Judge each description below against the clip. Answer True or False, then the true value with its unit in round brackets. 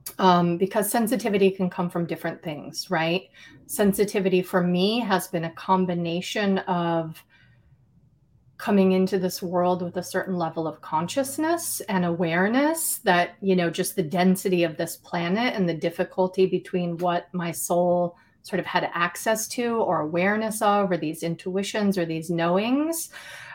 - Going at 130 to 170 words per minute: True (150 wpm)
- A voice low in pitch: False (180 Hz)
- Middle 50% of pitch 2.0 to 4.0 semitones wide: True (2.5 semitones)